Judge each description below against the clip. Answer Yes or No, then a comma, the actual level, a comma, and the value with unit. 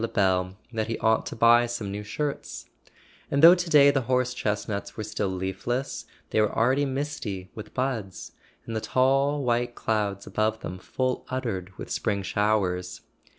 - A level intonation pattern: No, average, 4.4 semitones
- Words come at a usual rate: Yes, average, 165 wpm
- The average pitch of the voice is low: Yes, low, 110 Hz